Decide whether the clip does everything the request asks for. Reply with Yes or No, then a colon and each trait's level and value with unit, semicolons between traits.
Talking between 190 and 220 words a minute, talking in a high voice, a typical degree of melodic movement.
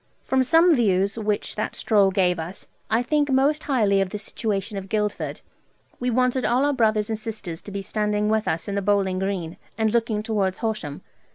Yes: average, 195 wpm; high, 210 Hz; average, 3.2 semitones